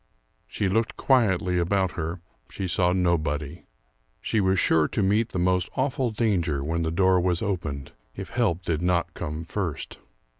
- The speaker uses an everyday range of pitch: Yes, average, 3.1 semitones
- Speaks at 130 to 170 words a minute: Yes, average, 160 wpm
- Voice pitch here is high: No, very low, 90 Hz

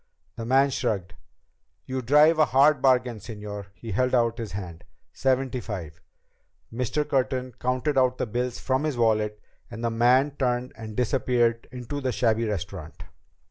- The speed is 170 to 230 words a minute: No, average, 155 wpm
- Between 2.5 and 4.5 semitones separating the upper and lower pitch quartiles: Yes, average, 3.1 semitones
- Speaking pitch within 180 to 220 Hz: No, low, 125 Hz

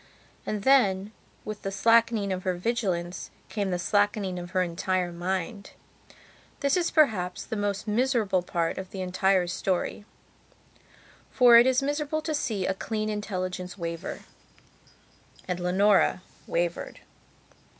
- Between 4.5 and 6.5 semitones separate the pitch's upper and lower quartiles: No, average, 3.5 semitones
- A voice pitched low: No, high, 195 Hz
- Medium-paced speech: No, slow, 130 wpm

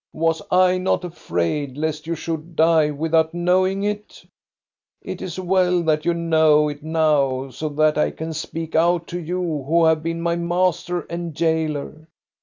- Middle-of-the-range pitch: Yes, medium, 165 Hz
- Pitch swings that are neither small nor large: No, narrow, 2.1 semitones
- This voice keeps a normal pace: Yes, average, 165 wpm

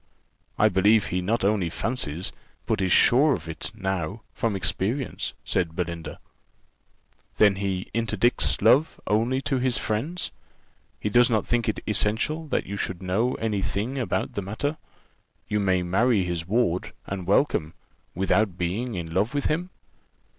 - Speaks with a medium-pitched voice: No, low, 105 Hz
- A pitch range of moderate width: Yes, average, 4.7 semitones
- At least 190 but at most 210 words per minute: No, average, 155 wpm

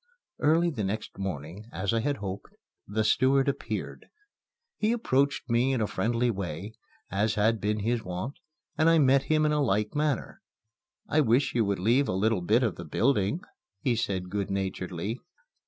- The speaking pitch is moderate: No, low, 110 Hz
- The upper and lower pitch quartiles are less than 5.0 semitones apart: No, wide, 5.5 semitones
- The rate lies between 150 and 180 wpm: Yes, average, 175 wpm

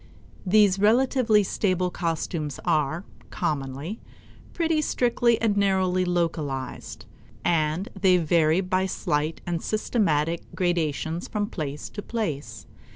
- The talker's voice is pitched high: No, medium, 180 Hz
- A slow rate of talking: Yes, slow, 105 wpm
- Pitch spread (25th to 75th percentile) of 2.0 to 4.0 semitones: No, average, 4.9 semitones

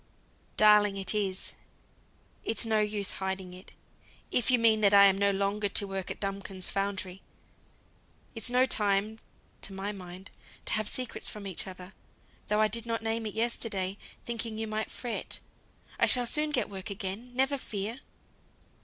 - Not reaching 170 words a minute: Yes, average, 160 wpm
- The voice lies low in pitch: No, high, 210 Hz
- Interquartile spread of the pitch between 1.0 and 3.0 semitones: Yes, narrow, 2.6 semitones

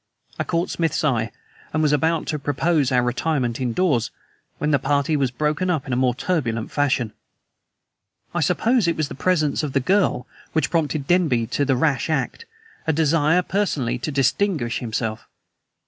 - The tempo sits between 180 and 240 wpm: No, average, 165 wpm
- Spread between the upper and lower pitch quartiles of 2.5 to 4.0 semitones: No, average, 4.4 semitones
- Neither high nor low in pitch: Yes, medium, 145 Hz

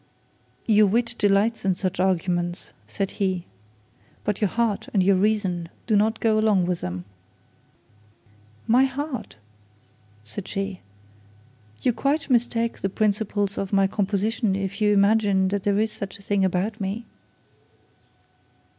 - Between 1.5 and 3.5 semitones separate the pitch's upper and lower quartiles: Yes, narrow, 2.5 semitones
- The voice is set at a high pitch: Yes, high, 200 Hz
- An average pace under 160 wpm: Yes, average, 140 wpm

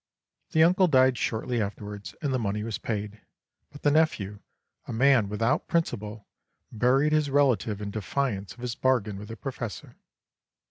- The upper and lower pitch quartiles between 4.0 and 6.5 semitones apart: Yes, average, 4.9 semitones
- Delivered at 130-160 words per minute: Yes, average, 155 wpm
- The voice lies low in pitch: Yes, low, 115 Hz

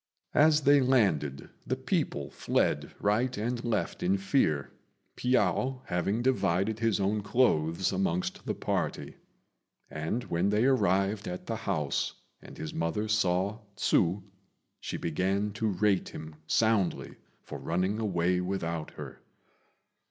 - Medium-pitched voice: No, low, 100 Hz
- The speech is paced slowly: Yes, slow, 130 wpm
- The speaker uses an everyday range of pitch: Yes, average, 4.1 semitones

